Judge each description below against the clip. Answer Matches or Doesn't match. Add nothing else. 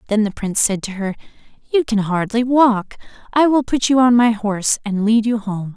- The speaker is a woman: Matches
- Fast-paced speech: Matches